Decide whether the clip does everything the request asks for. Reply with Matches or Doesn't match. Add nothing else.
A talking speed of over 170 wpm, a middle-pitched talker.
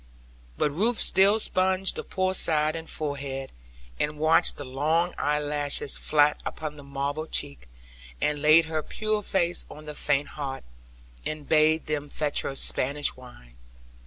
Doesn't match